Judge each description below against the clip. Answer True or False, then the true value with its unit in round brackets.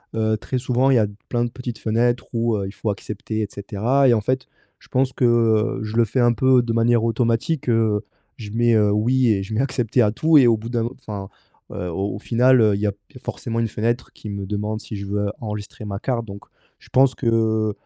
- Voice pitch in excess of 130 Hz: False (115 Hz)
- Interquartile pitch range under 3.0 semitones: True (2.5 semitones)